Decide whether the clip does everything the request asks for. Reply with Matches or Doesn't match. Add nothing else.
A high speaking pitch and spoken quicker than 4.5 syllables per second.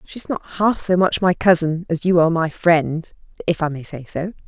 Doesn't match